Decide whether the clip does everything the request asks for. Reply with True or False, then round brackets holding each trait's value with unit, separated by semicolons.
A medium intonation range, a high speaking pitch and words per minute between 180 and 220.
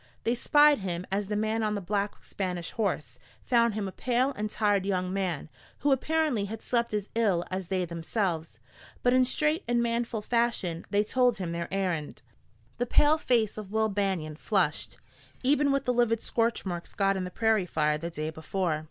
True (4.5 semitones; 205 Hz; 190 wpm)